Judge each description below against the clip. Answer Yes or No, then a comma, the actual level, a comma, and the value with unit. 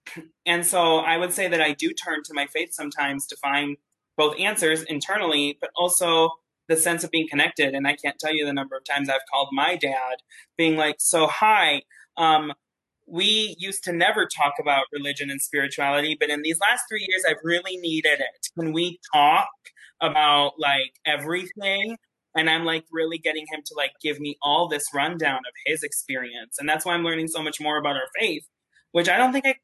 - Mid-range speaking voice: Yes, medium, 160 Hz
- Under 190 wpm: No, average, 200 wpm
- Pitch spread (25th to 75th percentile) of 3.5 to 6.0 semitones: No, average, 3.1 semitones